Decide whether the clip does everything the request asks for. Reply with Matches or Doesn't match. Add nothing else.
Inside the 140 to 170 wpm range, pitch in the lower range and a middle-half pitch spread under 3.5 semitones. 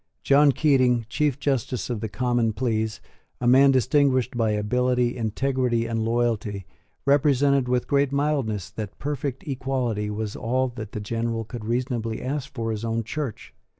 Matches